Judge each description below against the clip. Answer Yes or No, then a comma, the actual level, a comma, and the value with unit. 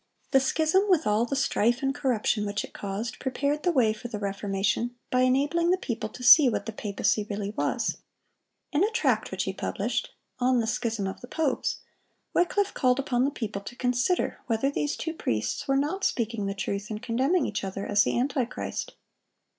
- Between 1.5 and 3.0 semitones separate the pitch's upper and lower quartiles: No, average, 5.0 semitones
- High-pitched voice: Yes, high, 245 Hz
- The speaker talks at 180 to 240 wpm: Yes, average, 195 wpm